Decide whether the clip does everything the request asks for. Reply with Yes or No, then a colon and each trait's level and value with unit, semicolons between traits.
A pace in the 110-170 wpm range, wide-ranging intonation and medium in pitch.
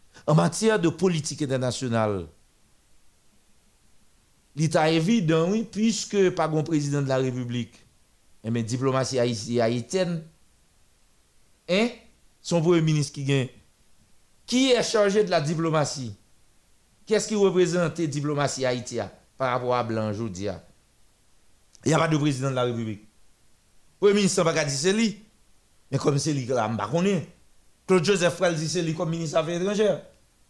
Yes: average, 150 wpm; wide, 6.7 semitones; medium, 155 Hz